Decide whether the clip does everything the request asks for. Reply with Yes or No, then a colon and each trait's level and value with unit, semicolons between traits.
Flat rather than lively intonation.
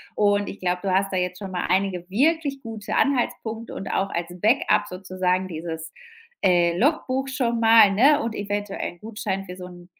No: average, 4.1 semitones